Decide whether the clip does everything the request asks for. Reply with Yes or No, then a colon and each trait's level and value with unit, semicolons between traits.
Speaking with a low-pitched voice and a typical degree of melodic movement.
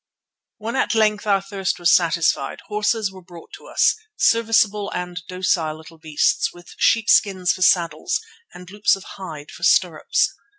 No: medium, 185 Hz; average, 3.3 semitones